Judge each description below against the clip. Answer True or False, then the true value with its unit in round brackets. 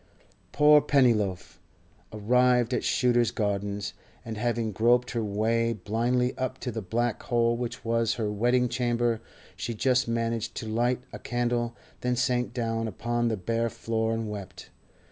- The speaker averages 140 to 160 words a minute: True (150 wpm)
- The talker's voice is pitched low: True (115 Hz)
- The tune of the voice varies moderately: False (1.6 semitones)